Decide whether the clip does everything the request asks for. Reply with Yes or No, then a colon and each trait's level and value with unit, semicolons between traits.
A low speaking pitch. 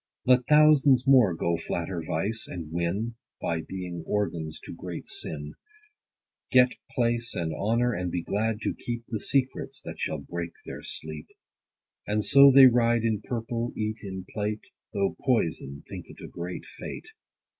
Yes: low, 105 Hz